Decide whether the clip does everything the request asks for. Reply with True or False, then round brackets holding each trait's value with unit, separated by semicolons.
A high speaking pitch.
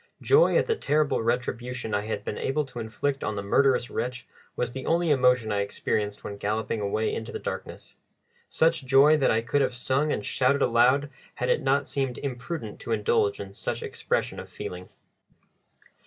False (125 Hz)